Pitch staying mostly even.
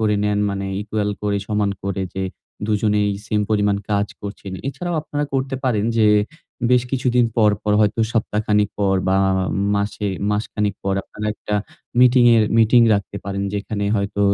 Yes: narrow, 1.7 semitones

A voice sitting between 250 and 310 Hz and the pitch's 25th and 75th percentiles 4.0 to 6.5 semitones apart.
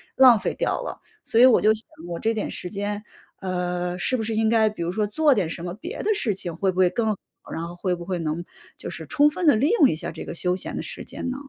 No: high, 205 Hz; average, 4.5 semitones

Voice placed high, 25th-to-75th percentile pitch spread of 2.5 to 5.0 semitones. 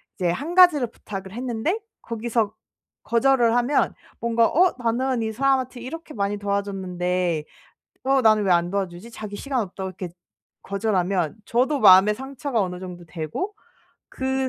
No: high, 220 Hz; wide, 5.5 semitones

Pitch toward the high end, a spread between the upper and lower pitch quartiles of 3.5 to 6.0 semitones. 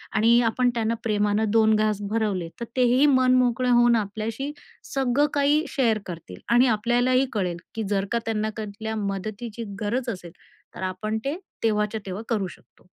No: high, 220 Hz; average, 2.8 semitones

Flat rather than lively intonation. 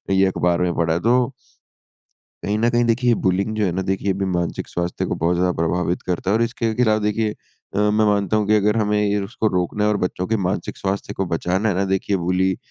No: average, 3.0 semitones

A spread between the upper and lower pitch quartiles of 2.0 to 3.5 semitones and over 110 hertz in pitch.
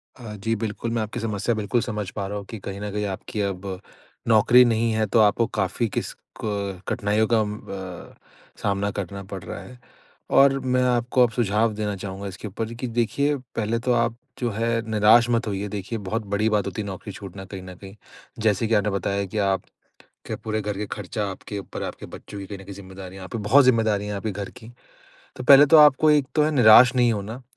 No: average, 2.8 semitones; low, 105 Hz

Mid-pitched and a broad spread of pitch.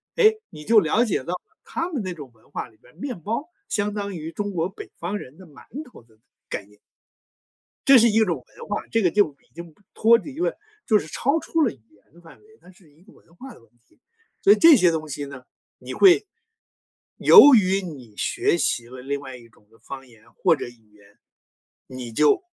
Yes: medium, 175 Hz; wide, 9.0 semitones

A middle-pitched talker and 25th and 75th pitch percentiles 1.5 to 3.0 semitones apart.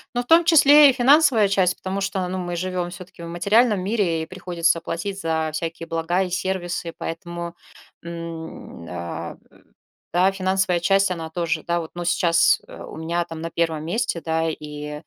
Yes: medium, 175 Hz; narrow, 2.6 semitones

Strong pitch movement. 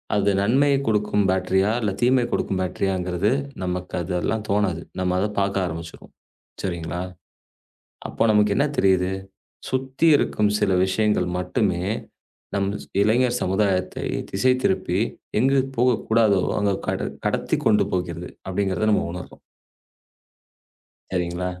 No: average, 2.9 semitones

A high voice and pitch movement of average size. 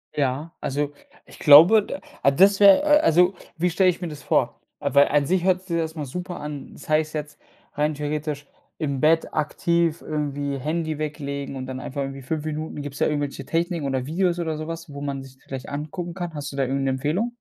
No: medium, 150 Hz; average, 3.1 semitones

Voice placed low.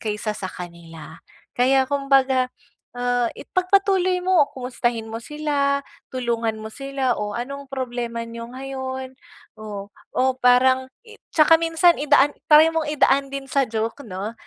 No: very high, 260 Hz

